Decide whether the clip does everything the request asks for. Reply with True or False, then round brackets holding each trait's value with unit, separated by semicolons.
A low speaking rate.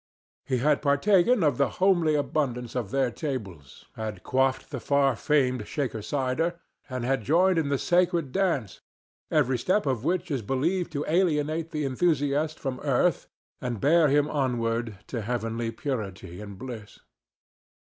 False (150 wpm)